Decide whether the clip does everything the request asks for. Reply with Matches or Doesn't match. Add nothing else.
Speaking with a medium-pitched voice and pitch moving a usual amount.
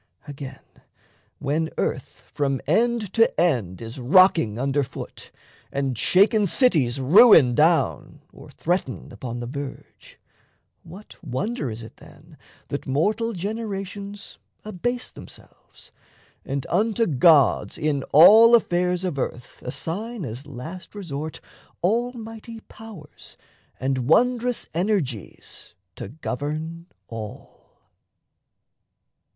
Doesn't match